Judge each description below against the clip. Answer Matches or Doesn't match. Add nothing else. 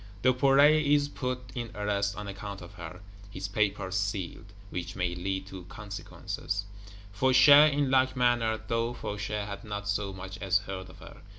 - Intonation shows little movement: Doesn't match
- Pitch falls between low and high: Doesn't match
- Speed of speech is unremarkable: Matches